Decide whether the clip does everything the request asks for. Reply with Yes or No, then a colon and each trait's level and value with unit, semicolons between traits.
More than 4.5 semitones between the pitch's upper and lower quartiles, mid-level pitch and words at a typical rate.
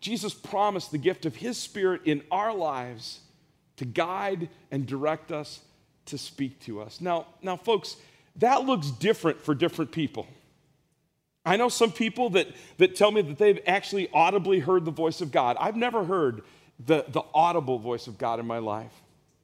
Yes: average, 5.3 semitones; medium, 165 Hz; average, 175 wpm